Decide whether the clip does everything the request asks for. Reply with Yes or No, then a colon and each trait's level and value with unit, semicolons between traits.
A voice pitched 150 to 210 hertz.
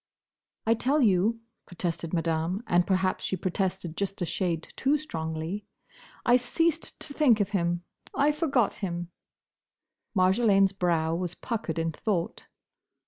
Yes: high, 190 Hz